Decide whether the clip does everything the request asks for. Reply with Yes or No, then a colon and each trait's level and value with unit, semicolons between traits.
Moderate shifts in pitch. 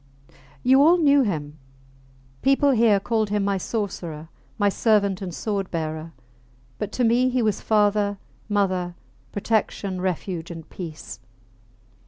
Yes: average, 4.1 semitones